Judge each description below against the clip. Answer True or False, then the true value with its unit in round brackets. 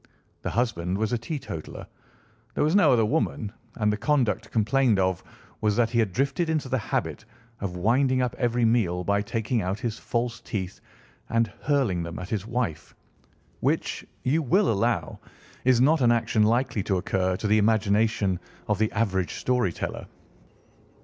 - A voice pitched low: True (115 Hz)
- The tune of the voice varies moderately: True (3.8 semitones)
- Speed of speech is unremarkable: True (170 wpm)